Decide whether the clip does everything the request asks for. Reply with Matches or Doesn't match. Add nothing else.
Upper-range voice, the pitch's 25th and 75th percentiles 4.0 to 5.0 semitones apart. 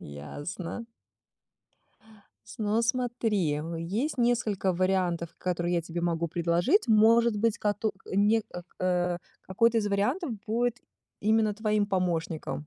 Matches